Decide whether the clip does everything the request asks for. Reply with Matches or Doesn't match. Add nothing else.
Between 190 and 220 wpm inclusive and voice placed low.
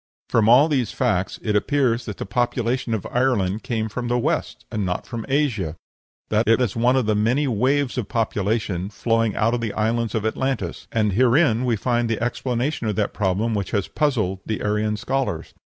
Matches